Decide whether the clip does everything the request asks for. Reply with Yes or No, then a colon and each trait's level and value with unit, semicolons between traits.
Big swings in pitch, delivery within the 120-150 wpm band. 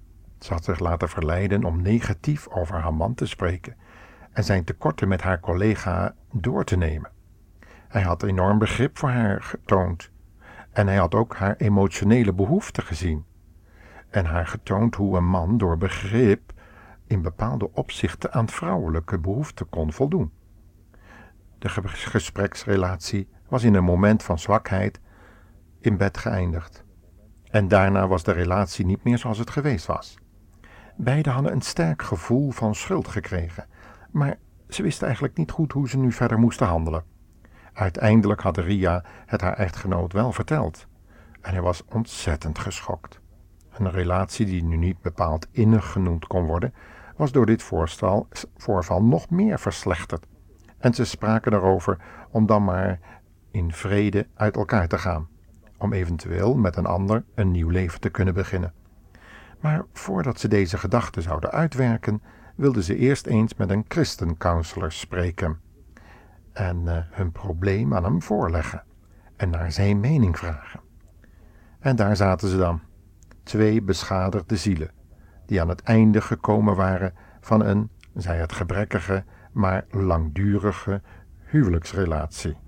No: average, 3.7 semitones; average, 145 wpm